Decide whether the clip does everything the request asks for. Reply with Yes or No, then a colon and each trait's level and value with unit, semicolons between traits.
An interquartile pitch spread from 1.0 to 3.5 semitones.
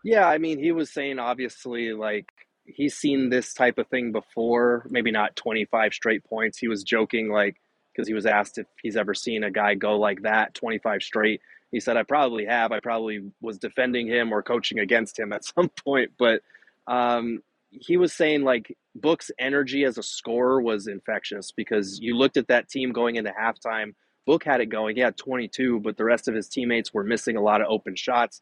Yes: average, 3.0 semitones